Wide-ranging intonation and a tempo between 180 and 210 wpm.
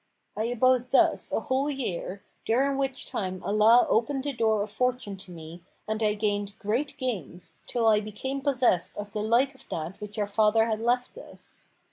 No: average, 3.8 semitones; average, 185 wpm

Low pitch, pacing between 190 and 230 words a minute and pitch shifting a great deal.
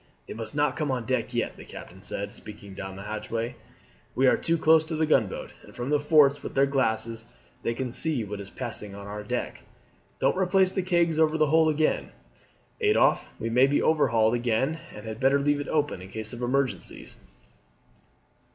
Yes: low, 130 Hz; average, 195 wpm; wide, 5.7 semitones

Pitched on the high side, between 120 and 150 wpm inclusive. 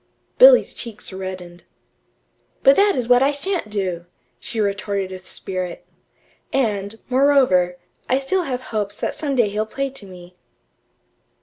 Yes: high, 215 Hz; average, 140 wpm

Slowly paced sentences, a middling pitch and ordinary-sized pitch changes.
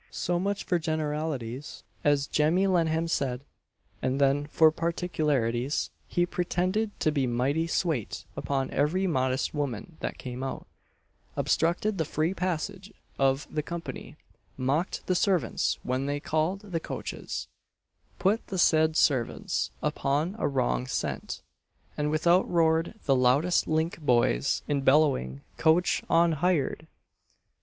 Yes: slow, 130 wpm; medium, 155 Hz; average, 4.1 semitones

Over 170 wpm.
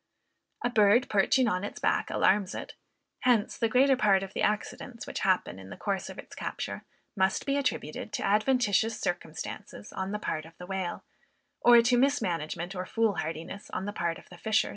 Yes: average, 185 wpm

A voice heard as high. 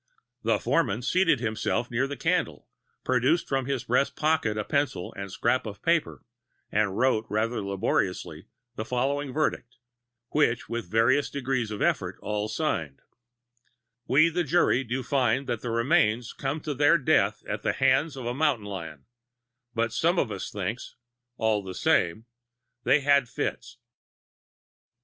No: low, 125 Hz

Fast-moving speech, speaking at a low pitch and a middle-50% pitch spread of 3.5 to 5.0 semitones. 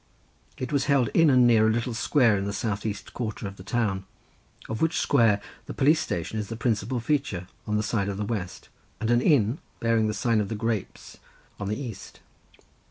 No: fast, 210 wpm; low, 110 Hz; average, 3.0 semitones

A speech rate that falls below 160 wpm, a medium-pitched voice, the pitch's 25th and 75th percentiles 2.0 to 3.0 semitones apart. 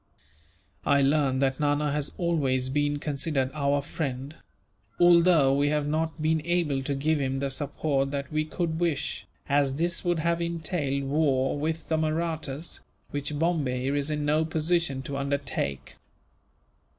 Yes: average, 150 wpm; medium, 145 Hz; narrow, 2.6 semitones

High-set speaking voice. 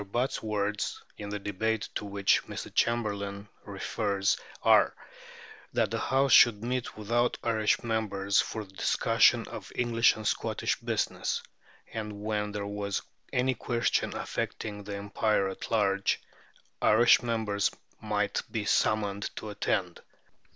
No: low, 105 Hz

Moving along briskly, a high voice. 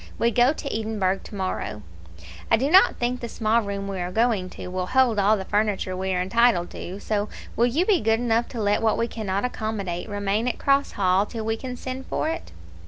Yes: fast, 220 wpm; high, 220 Hz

